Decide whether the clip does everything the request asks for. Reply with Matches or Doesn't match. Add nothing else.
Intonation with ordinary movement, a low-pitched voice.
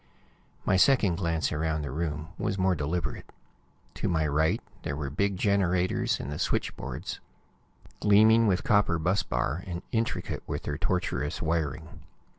Matches